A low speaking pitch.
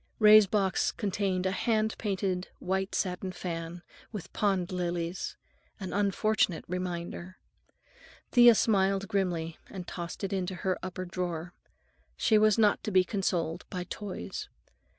No: medium, 185 Hz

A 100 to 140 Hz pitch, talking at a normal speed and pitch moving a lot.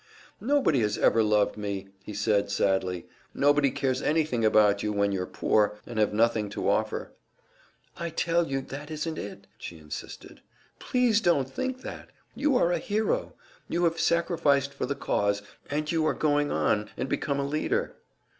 Yes: low, 135 Hz; average, 175 wpm; wide, 7.7 semitones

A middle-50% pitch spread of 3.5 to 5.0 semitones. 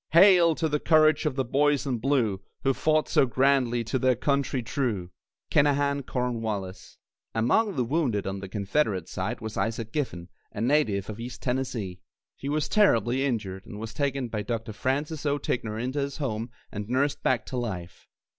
Yes: average, 4.5 semitones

